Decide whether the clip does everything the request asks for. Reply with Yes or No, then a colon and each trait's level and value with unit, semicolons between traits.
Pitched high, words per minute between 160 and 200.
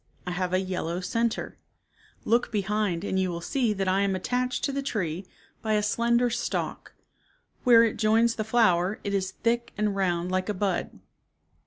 Yes: high, 205 Hz; average, 180 wpm